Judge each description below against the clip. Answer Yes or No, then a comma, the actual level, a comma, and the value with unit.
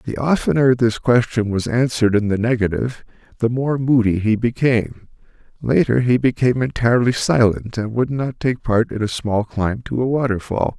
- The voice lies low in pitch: Yes, low, 115 Hz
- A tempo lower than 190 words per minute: Yes, average, 170 wpm